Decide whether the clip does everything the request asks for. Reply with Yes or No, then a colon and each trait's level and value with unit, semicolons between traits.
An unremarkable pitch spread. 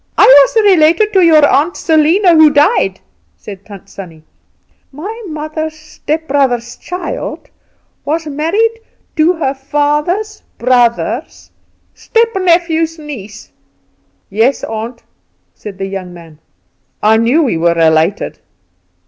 No: wide, 6.8 semitones